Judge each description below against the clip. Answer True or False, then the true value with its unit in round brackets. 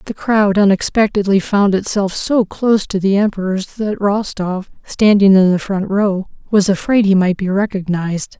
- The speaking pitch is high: True (200 Hz)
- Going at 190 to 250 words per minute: False (165 wpm)